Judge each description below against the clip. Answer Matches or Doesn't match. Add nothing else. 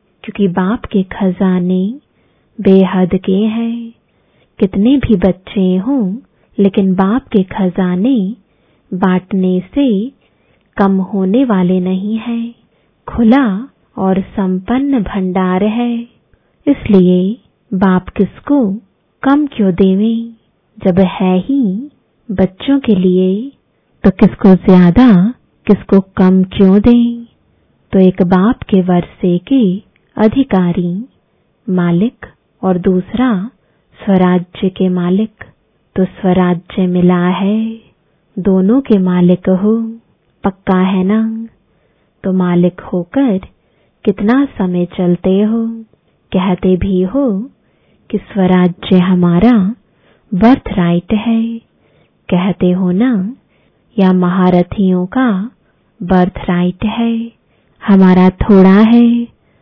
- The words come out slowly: Matches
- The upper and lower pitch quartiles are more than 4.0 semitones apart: Doesn't match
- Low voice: Doesn't match